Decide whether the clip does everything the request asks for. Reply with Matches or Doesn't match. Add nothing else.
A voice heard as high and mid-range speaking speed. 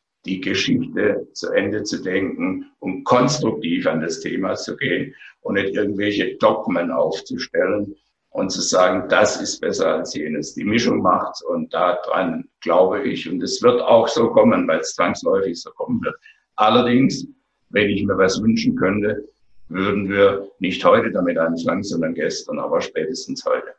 Matches